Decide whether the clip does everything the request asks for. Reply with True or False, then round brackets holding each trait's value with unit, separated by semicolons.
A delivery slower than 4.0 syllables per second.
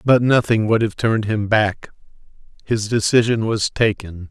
False (4.6 syllables/s)